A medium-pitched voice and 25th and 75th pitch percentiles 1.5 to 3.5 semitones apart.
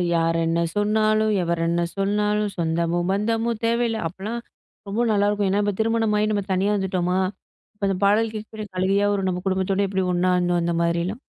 No: high, 200 Hz; average, 2.9 semitones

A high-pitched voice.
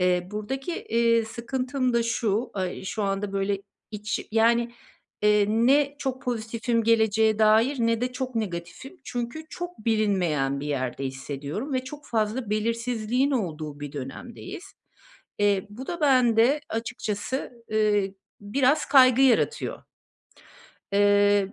Yes: high, 225 Hz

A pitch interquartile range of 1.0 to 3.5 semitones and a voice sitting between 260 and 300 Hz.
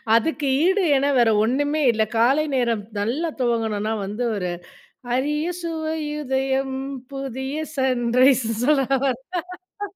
No: average, 4.1 semitones; very high, 265 Hz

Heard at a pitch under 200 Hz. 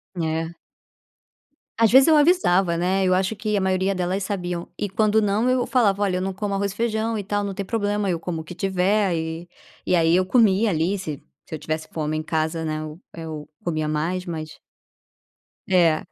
Yes: medium, 185 Hz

